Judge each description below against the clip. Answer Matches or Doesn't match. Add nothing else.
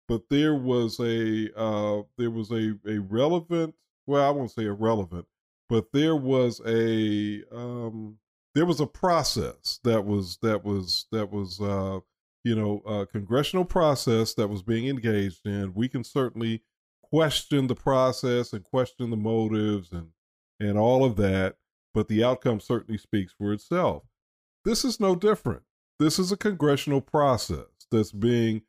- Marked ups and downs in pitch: Doesn't match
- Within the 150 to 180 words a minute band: Matches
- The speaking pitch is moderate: Doesn't match